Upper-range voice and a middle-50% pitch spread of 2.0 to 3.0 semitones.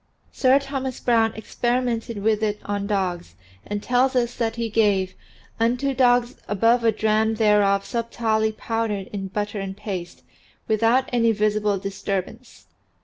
Yes: high, 220 Hz; narrow, 2.6 semitones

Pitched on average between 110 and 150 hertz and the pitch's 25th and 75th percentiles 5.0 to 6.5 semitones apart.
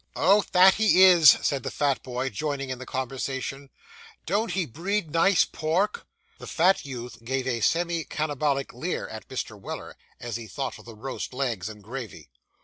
Yes: low, 135 Hz; wide, 5.4 semitones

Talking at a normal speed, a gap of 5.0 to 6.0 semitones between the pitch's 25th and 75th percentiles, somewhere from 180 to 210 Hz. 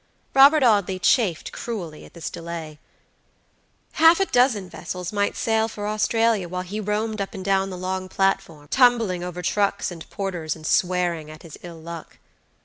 No: average, 165 wpm; average, 4.0 semitones; high, 190 Hz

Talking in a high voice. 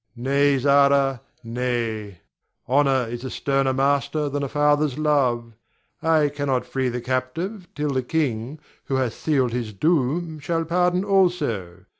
No: medium, 140 Hz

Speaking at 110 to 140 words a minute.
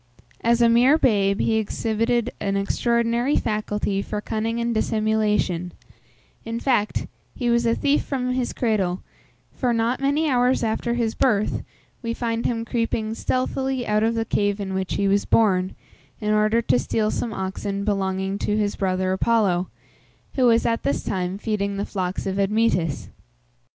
No: average, 160 wpm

